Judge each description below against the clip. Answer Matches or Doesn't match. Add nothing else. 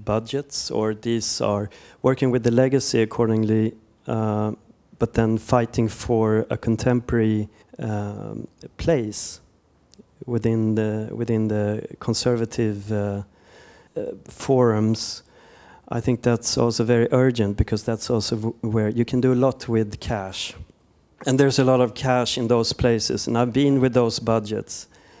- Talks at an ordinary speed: Matches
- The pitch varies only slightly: Matches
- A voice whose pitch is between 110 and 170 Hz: Matches